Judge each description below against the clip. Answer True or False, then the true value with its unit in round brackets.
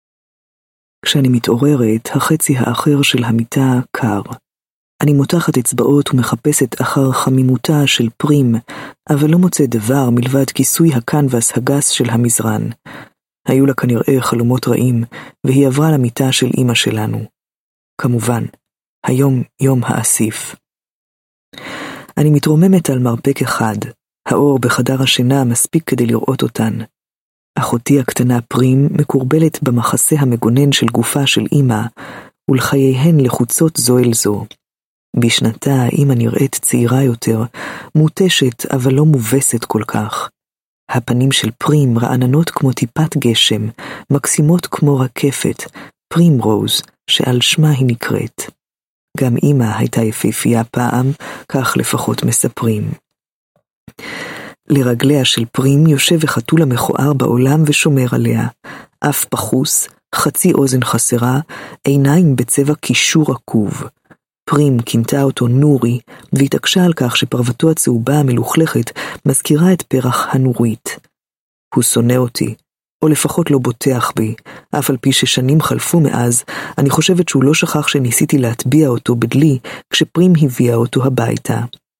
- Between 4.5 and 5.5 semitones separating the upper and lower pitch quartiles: False (3.4 semitones)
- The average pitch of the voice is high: False (130 Hz)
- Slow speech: False (120 wpm)